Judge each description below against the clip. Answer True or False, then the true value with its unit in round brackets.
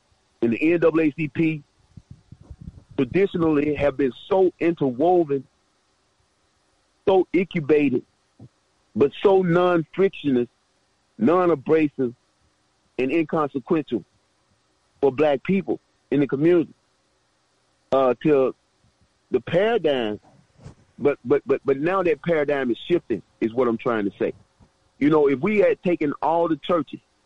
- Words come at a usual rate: False (115 wpm)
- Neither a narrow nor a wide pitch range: True (4.4 semitones)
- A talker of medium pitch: True (150 Hz)